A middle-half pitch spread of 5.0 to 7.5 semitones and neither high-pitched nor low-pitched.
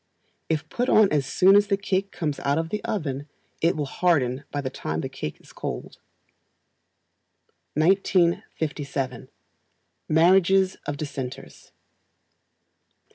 Yes: average, 5.3 semitones; medium, 160 Hz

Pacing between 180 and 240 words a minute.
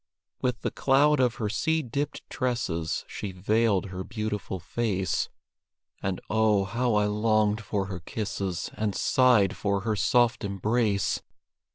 No: average, 140 wpm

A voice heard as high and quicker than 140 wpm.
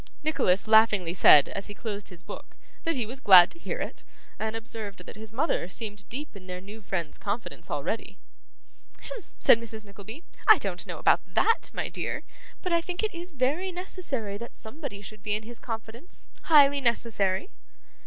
Yes: high, 225 Hz; average, 185 wpm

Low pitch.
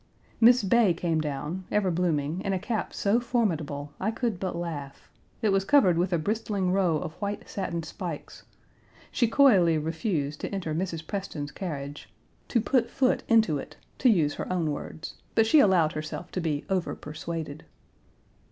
No: medium, 180 Hz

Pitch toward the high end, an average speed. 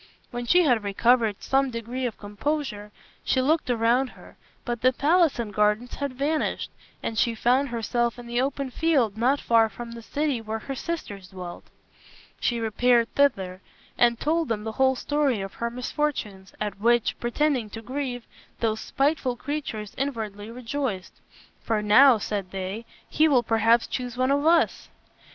Yes: high, 240 Hz; average, 165 wpm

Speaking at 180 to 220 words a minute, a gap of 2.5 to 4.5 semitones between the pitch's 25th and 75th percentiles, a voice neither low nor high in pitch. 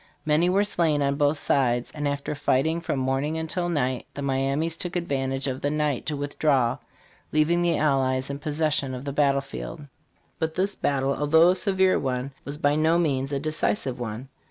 Yes: average, 185 wpm; average, 2.9 semitones; medium, 145 Hz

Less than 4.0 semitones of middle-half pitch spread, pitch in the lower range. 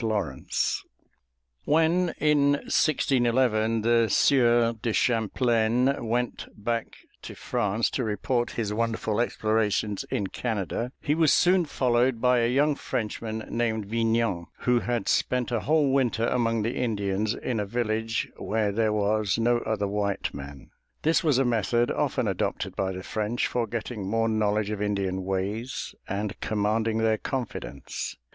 Yes: narrow, 2.6 semitones; low, 115 Hz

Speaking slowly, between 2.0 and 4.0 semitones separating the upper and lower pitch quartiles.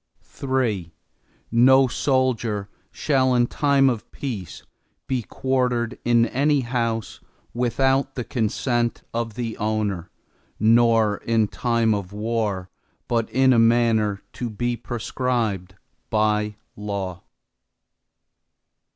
Yes: slow, 105 wpm; average, 2.9 semitones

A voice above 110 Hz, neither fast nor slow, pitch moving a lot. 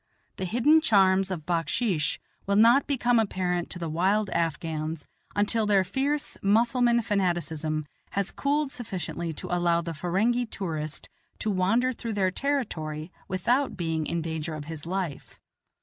Yes: high, 190 Hz; average, 145 wpm; wide, 5.8 semitones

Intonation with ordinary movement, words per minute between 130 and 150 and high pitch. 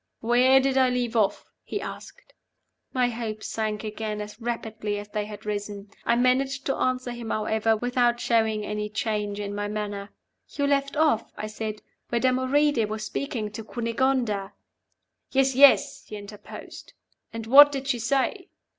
No: average, 3.5 semitones; average, 165 wpm; high, 230 Hz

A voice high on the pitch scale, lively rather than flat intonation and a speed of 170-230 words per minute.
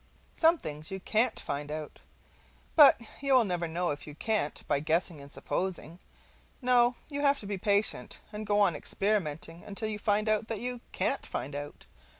Yes: high, 200 Hz; wide, 6.0 semitones; average, 175 wpm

